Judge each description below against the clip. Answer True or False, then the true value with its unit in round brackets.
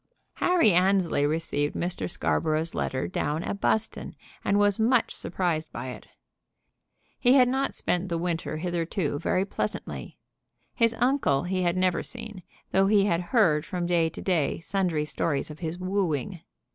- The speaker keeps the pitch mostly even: False (3.9 semitones)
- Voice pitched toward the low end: False (180 Hz)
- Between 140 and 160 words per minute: True (155 wpm)